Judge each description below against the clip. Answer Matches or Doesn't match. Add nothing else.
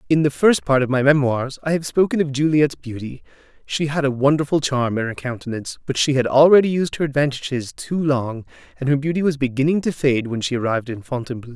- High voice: Doesn't match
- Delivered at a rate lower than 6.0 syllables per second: Doesn't match